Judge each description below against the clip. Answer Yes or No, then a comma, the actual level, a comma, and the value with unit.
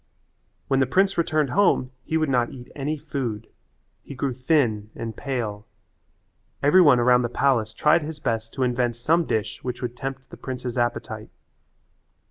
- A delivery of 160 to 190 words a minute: Yes, average, 165 wpm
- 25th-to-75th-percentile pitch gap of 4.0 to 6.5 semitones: No, average, 3.4 semitones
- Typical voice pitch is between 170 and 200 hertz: No, low, 130 Hz